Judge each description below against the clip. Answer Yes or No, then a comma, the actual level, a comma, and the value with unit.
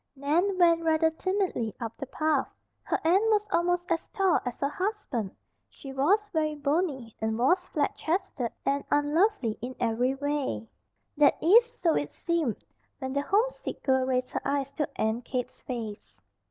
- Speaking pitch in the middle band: No, very high, 290 Hz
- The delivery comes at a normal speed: Yes, average, 165 wpm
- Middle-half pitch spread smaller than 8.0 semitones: Yes, wide, 5.5 semitones